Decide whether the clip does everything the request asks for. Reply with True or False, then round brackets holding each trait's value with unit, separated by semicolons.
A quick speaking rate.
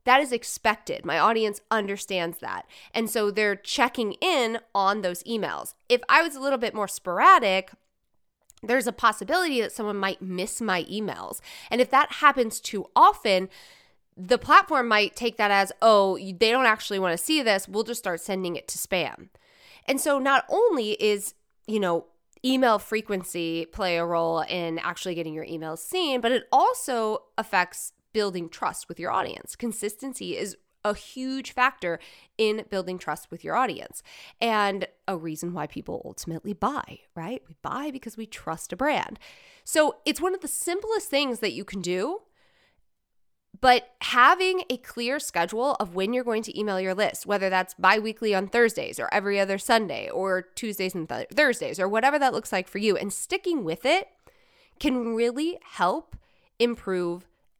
False (175 wpm)